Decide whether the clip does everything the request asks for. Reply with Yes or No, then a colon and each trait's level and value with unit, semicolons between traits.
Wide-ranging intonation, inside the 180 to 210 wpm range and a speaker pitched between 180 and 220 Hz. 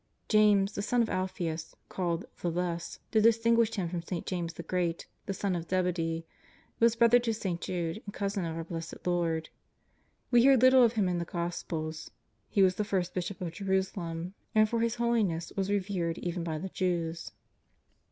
No: average, 3.9 semitones; average, 190 wpm; medium, 185 Hz